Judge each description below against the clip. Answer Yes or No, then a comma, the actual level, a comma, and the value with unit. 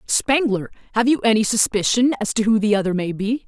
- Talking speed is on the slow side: No, fast, 205 wpm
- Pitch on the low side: No, high, 220 Hz